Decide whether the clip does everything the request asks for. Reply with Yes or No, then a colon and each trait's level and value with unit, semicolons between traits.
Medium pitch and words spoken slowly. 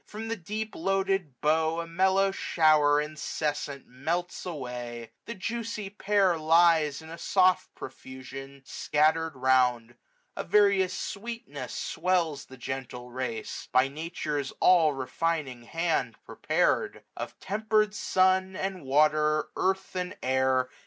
Yes: medium, 160 Hz; slow, 125 wpm